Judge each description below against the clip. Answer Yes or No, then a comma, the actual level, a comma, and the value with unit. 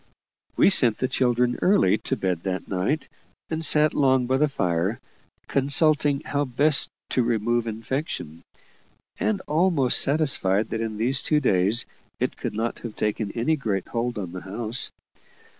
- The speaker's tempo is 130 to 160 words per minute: Yes, average, 155 wpm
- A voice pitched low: Yes, low, 120 Hz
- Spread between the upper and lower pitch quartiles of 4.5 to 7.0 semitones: Yes, average, 5.2 semitones